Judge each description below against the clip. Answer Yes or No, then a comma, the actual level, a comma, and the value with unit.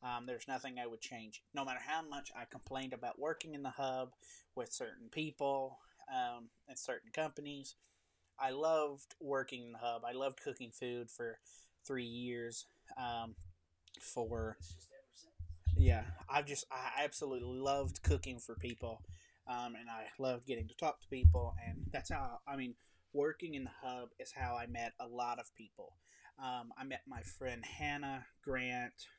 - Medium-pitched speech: No, low, 120 Hz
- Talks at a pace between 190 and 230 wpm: No, average, 165 wpm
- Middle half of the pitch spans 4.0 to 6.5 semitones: No, average, 3.3 semitones